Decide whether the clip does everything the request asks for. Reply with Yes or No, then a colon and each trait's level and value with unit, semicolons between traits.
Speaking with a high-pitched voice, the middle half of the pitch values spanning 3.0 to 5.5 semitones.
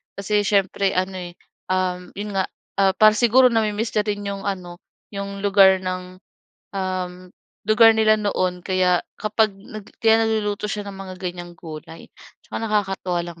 No: high, 195 Hz; narrow, 2.4 semitones